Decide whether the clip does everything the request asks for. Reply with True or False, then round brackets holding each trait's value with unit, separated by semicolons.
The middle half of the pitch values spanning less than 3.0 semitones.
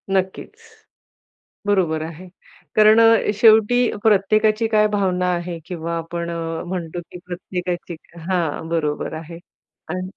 False (3.5 semitones)